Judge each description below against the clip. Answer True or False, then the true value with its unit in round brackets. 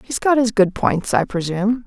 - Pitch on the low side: False (210 Hz)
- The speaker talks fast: True (225 wpm)